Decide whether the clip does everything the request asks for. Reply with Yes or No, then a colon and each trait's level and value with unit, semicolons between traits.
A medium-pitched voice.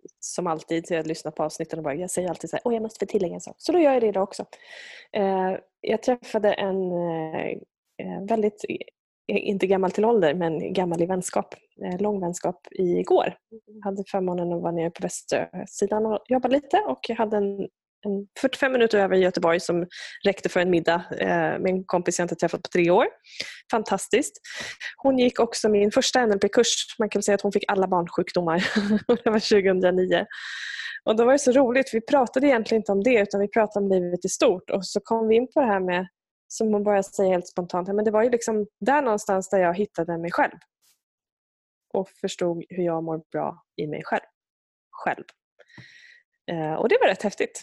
No: high, 200 Hz